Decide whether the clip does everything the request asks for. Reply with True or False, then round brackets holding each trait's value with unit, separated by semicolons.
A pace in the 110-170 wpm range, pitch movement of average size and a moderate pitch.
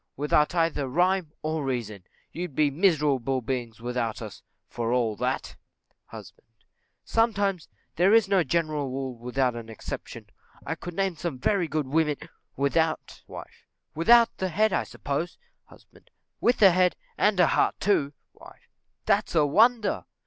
False (150 wpm; 5.9 semitones; 155 Hz)